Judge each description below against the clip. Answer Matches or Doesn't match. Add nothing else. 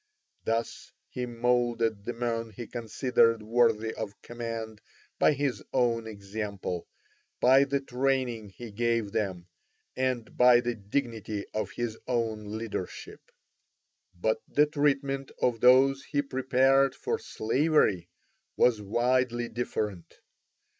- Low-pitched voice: Matches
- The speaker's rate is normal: Doesn't match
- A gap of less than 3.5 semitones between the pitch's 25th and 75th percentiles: Matches